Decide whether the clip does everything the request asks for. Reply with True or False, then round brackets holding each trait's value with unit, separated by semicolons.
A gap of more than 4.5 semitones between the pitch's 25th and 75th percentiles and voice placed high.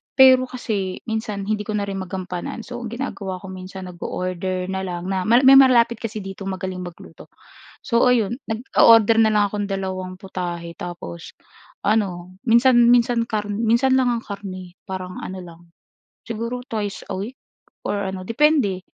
False (3.8 semitones; 200 Hz)